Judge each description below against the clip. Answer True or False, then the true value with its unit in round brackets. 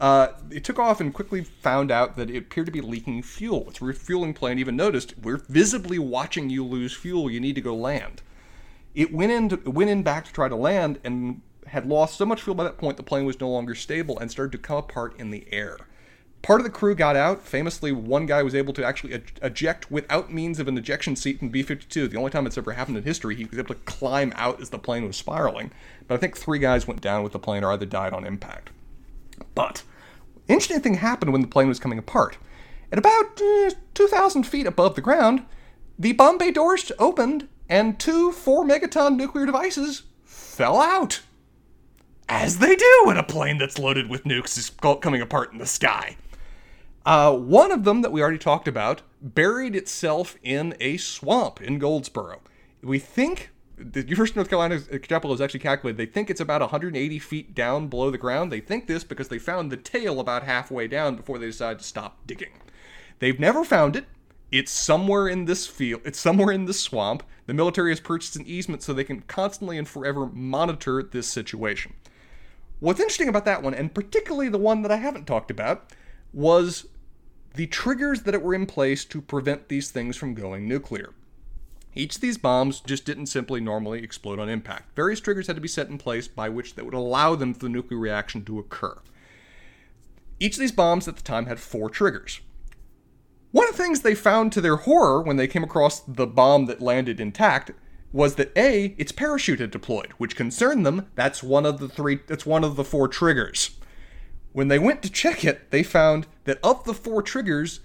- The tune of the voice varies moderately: False (7.2 semitones)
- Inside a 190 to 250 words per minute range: True (205 wpm)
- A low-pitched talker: False (145 Hz)